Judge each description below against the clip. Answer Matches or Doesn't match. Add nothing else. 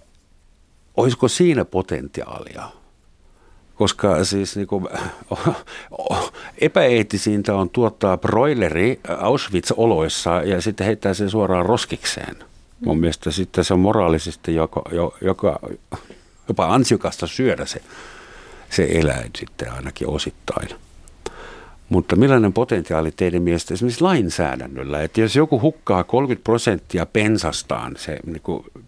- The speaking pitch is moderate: Doesn't match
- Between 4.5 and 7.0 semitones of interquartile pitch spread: Matches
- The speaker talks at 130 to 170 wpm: Doesn't match